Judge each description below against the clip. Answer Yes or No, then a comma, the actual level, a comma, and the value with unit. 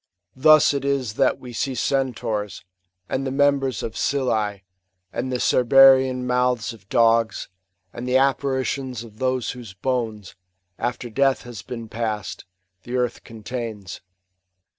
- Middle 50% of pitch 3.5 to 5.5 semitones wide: No, average, 2.7 semitones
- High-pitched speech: No, low, 125 Hz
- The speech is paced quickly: No, average, 140 wpm